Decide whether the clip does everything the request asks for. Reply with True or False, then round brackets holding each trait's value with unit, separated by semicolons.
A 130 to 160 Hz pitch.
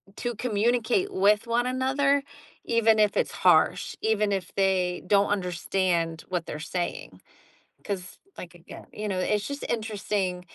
False (205 Hz)